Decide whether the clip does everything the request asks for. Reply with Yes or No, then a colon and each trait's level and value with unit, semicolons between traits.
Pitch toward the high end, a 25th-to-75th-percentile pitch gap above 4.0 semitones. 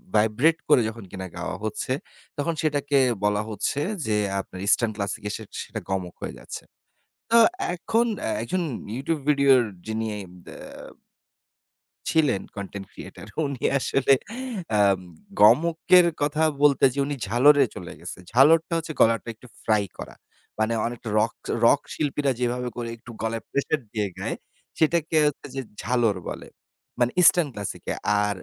No: low, 125 Hz; wide, 5.5 semitones